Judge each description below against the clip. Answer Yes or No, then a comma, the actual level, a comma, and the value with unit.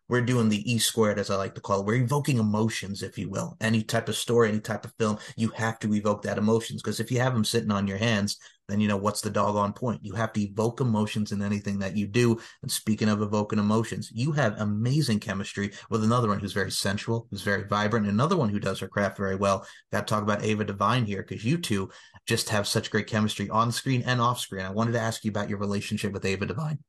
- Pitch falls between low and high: No, low, 105 Hz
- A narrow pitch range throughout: Yes, narrow, 2.1 semitones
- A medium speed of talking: No, fast, 255 wpm